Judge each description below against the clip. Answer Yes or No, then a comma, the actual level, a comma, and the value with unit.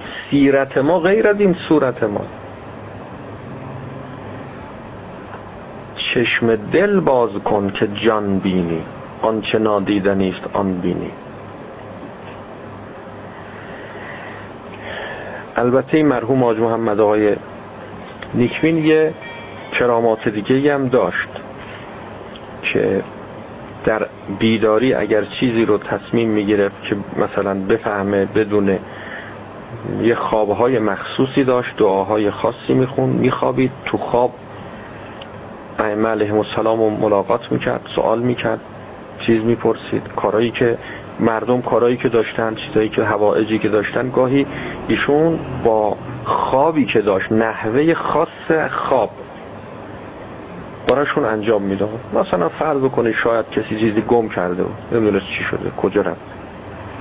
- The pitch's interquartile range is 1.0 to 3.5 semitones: Yes, average, 3.2 semitones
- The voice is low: Yes, low, 110 Hz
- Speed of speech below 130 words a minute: Yes, slow, 105 wpm